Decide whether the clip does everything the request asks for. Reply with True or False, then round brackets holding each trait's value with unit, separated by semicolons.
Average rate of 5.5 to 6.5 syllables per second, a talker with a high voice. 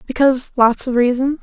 True (5.8 syllables/s; 255 Hz)